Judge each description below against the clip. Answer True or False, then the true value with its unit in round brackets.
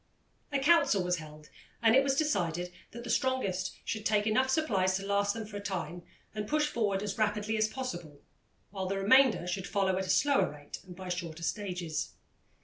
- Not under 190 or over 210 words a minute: True (195 wpm)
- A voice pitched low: False (200 Hz)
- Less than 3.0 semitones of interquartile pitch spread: False (4.5 semitones)